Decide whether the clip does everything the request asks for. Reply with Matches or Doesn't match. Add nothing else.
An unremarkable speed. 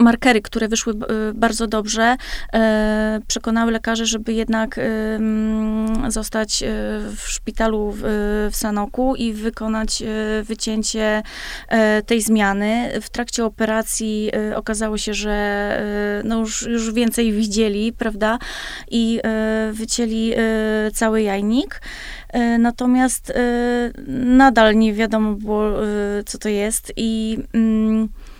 Doesn't match